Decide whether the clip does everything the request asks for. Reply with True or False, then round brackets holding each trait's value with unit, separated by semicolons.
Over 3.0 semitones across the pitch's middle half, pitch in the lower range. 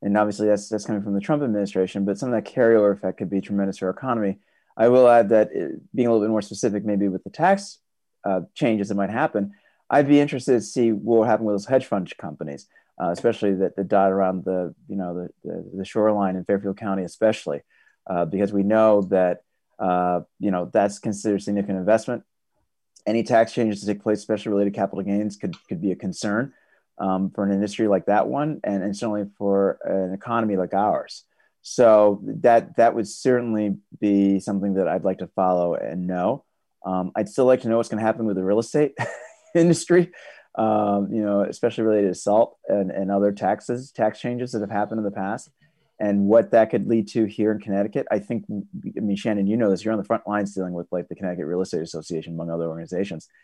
False (2.7 semitones; 105 Hz)